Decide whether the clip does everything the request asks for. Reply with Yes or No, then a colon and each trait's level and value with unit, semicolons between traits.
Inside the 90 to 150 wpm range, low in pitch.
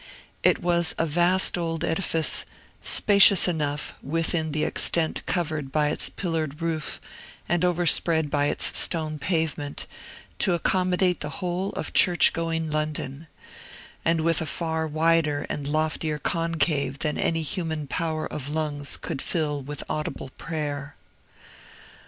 No: slow, 135 wpm; medium, 160 Hz